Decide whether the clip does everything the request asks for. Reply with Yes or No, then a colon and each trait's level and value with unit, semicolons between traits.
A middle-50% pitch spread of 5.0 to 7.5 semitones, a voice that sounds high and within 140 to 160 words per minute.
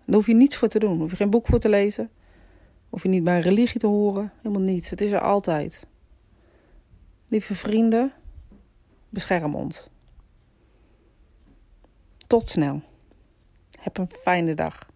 Yes: wide, 5.4 semitones; high, 200 Hz; average, 150 wpm